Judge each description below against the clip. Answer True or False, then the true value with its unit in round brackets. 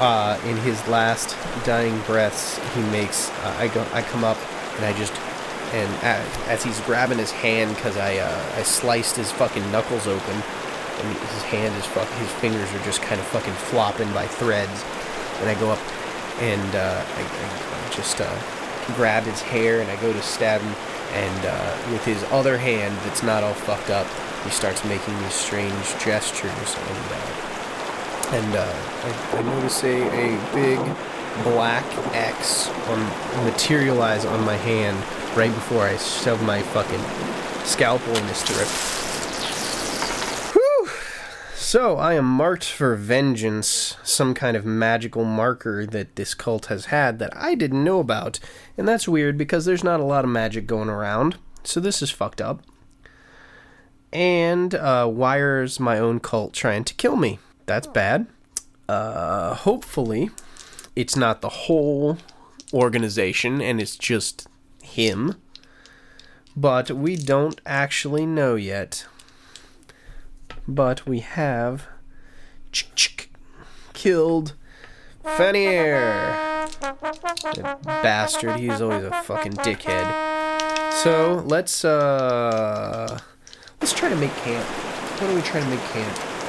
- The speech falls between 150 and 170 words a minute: False (140 wpm)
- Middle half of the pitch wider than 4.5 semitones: True (5.6 semitones)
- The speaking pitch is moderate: False (120 Hz)